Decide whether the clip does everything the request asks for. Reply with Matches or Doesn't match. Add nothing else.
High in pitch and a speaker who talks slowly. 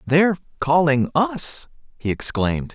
Doesn't match